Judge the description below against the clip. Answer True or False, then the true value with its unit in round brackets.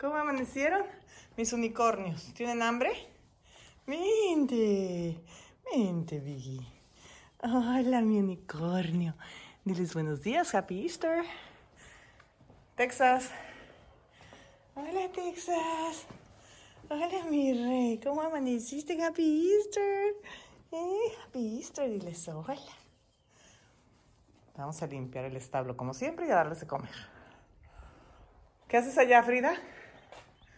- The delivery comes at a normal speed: False (90 wpm)